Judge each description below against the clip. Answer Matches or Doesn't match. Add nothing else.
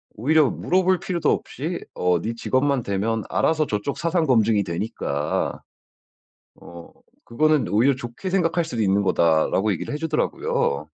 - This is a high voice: Doesn't match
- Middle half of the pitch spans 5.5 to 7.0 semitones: Doesn't match